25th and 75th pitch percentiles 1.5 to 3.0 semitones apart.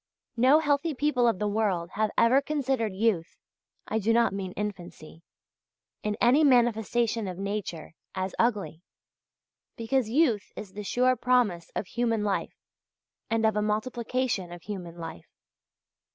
No: average, 4.0 semitones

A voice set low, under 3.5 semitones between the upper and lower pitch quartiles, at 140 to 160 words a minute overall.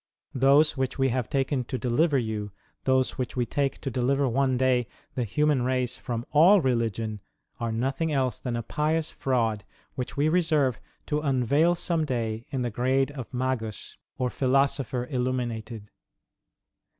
Yes: low, 130 Hz; narrow, 2.6 semitones; average, 155 wpm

